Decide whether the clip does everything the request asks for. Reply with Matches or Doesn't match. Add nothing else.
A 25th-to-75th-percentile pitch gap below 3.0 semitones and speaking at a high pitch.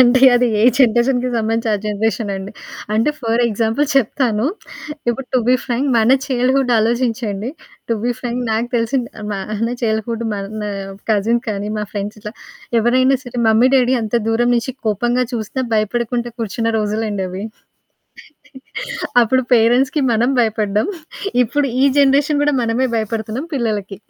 Matches